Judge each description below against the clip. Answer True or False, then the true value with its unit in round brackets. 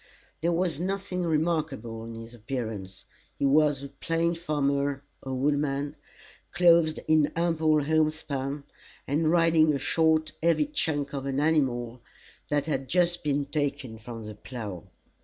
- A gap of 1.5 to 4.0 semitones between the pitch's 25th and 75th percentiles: True (3.2 semitones)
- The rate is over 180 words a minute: False (140 wpm)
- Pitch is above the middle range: False (145 Hz)